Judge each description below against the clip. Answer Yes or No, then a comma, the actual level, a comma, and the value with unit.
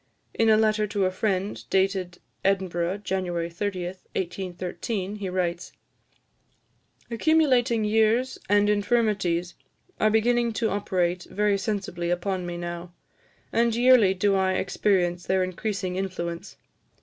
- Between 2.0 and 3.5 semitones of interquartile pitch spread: Yes, average, 3.0 semitones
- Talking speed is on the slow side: Yes, slow, 120 wpm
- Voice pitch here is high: Yes, high, 195 Hz